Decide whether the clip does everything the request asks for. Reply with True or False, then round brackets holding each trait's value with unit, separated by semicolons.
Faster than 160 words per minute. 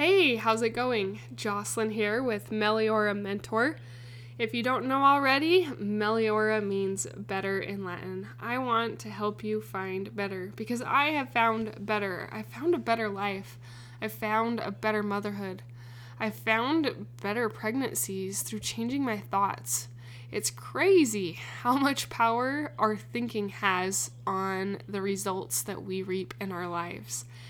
False (145 wpm)